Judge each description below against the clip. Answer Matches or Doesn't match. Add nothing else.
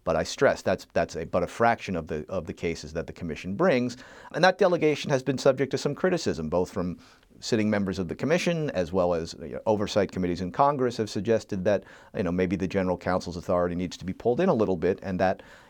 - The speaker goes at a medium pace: Doesn't match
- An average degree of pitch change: Doesn't match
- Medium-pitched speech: Doesn't match